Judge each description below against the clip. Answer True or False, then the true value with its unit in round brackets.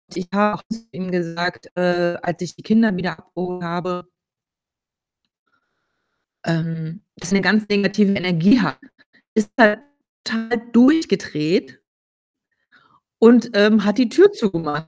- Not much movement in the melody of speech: False (3.8 semitones)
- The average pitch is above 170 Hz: True (190 Hz)